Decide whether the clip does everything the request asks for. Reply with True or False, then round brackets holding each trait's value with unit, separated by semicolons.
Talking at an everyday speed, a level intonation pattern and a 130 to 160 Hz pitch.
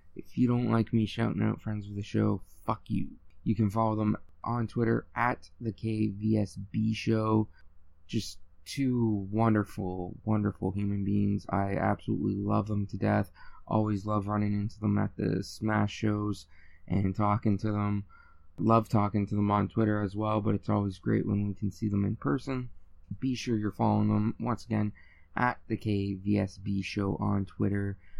False (170 wpm; 1.7 semitones; 105 Hz)